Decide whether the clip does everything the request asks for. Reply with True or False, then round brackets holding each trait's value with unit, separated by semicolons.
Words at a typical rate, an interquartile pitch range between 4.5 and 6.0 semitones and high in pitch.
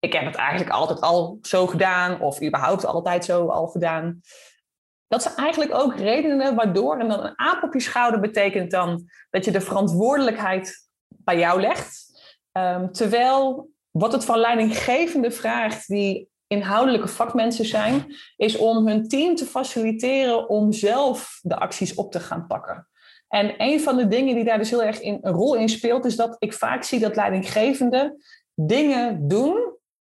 True (170 wpm; 4.8 semitones; 225 Hz)